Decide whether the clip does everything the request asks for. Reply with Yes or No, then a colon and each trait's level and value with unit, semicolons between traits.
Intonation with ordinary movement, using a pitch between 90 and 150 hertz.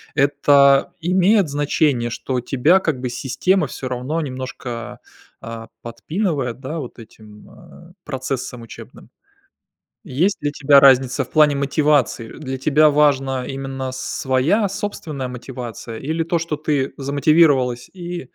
Yes: average, 3.4 semitones; medium, 140 Hz